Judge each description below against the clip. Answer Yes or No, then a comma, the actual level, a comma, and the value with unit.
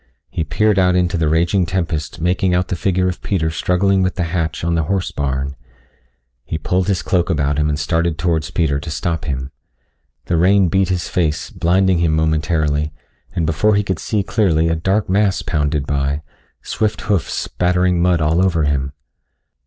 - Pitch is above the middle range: No, very low, 85 Hz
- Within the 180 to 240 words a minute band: Yes, average, 185 wpm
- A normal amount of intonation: Yes, average, 3.0 semitones